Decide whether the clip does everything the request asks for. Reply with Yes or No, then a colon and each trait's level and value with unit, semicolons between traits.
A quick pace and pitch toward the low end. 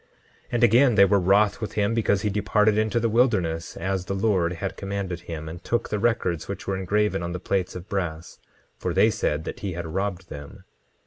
Yes: fast, 210 wpm; low, 100 Hz